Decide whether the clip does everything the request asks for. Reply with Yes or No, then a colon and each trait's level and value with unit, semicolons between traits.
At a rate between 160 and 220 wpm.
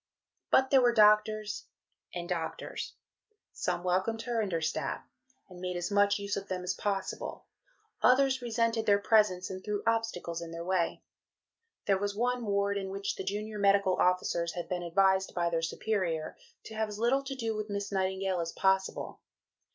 Yes: average, 175 wpm